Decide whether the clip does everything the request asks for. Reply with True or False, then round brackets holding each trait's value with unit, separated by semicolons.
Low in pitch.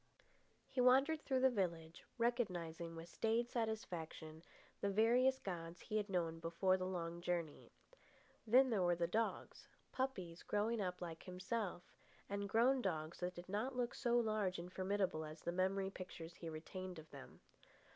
False (185 Hz)